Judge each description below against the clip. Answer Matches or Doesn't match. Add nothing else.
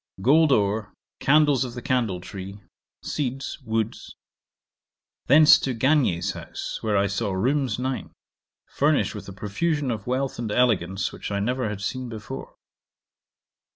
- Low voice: Matches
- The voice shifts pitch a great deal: Doesn't match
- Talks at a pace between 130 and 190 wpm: Matches